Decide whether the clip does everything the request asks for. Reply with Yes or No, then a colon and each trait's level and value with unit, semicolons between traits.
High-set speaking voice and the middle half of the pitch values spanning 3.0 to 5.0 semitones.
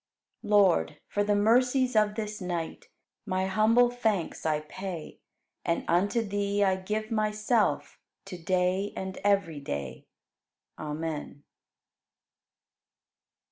Yes: high, 200 Hz; average, 3.7 semitones